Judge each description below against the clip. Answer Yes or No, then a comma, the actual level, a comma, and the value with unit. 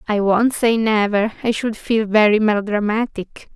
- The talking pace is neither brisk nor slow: Yes, average, 150 wpm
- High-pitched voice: Yes, high, 215 Hz